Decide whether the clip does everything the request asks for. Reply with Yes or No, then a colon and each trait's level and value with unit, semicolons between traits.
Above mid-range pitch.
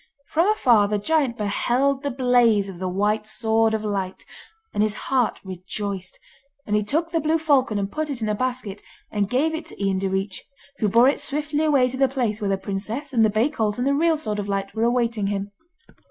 Yes: high, 225 Hz